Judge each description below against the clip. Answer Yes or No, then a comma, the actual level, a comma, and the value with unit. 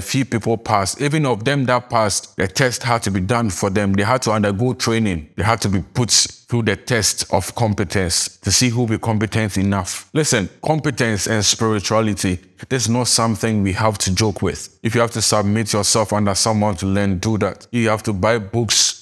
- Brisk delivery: Yes, fast, 210 wpm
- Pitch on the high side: No, low, 110 Hz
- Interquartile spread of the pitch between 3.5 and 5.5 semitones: No, average, 3.0 semitones